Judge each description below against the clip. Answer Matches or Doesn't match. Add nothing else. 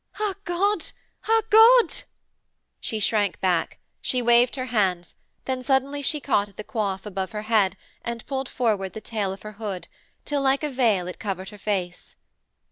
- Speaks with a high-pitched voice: Matches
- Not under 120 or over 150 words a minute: Doesn't match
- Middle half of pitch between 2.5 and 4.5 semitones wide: Doesn't match